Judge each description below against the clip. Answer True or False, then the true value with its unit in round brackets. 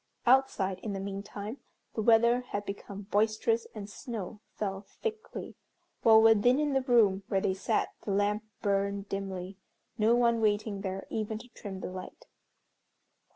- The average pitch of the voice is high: True (210 Hz)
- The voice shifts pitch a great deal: False (2.8 semitones)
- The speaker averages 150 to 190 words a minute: True (155 wpm)